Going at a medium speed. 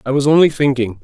No: fast, 230 wpm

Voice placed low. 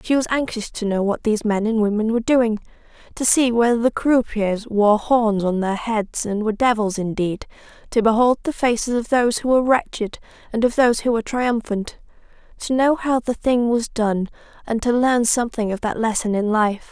No: high, 225 Hz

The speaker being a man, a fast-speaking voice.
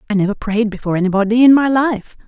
No: female; fast, 210 wpm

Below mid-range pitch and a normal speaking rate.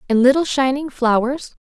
No: very high, 260 Hz; average, 145 wpm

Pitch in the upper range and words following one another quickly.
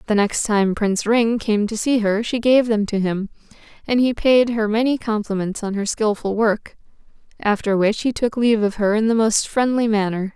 Yes: high, 215 Hz; fast, 210 wpm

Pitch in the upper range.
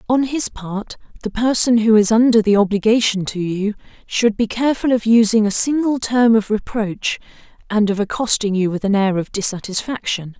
Yes: high, 215 Hz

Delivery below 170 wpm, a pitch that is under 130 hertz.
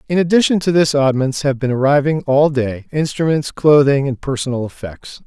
No: average, 160 wpm; medium, 140 Hz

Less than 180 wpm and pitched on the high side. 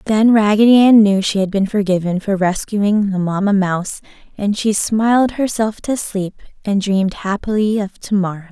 Yes: average, 170 wpm; high, 205 Hz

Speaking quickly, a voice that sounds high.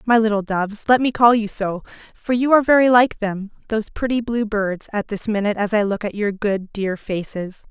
Yes: fast, 220 wpm; high, 215 Hz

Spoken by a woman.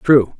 No: male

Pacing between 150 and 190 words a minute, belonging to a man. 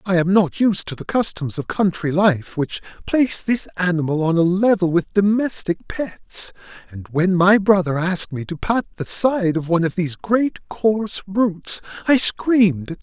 No: average, 200 wpm; male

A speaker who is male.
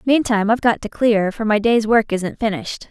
No: female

